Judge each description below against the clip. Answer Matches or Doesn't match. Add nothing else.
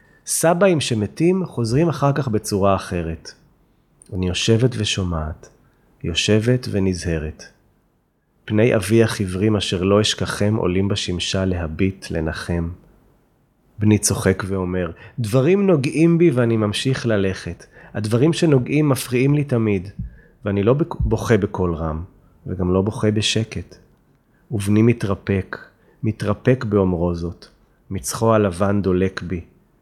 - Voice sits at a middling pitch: Doesn't match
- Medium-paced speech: Matches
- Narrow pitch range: Doesn't match